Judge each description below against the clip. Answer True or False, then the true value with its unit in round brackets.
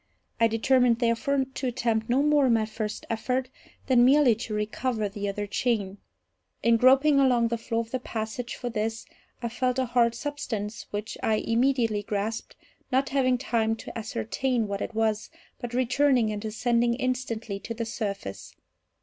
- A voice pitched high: True (230 Hz)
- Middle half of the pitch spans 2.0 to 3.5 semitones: True (2.6 semitones)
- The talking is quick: False (165 wpm)